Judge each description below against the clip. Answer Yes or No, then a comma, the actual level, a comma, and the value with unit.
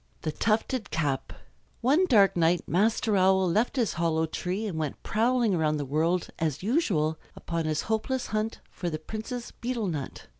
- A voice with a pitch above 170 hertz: Yes, high, 190 Hz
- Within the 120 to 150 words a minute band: No, average, 165 wpm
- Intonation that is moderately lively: No, wide, 5.9 semitones